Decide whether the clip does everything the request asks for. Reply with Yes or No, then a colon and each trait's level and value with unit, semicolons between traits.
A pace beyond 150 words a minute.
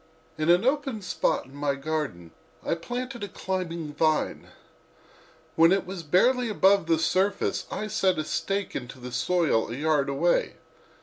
Yes: average, 160 wpm